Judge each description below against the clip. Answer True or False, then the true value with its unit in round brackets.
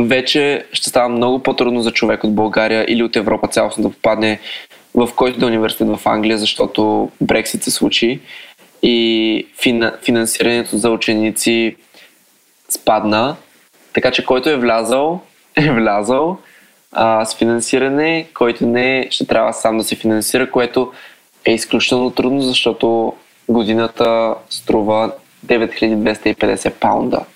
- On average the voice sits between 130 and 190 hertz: False (115 Hz)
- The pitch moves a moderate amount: False (2.2 semitones)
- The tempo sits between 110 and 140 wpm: True (125 wpm)